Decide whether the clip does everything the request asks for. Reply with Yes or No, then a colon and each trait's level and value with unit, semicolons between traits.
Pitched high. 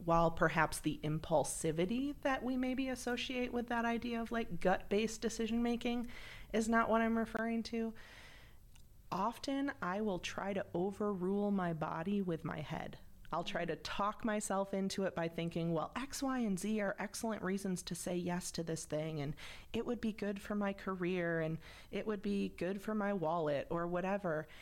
Yes: high, 200 Hz